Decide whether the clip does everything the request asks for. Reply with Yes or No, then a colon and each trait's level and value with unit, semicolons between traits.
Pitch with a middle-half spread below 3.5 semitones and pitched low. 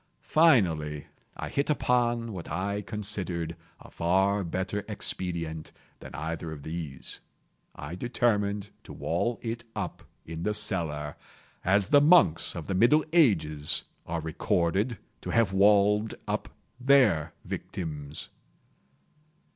No: average, 5.2 semitones; very low, 95 Hz